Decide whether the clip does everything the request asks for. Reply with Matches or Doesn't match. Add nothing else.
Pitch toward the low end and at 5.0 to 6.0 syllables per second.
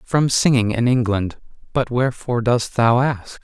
Doesn't match